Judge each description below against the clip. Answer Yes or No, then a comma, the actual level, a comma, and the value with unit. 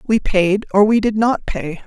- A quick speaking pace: Yes, fast, 225 wpm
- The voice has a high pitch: Yes, high, 205 Hz